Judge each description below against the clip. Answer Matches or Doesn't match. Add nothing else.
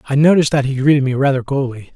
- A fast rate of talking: Matches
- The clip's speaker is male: Matches